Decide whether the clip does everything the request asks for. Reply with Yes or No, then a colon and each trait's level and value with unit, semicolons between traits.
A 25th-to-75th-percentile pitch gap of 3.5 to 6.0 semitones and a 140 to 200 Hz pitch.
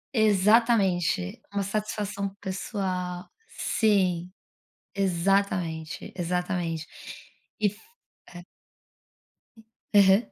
No: narrow, 2.5 semitones; high, 190 Hz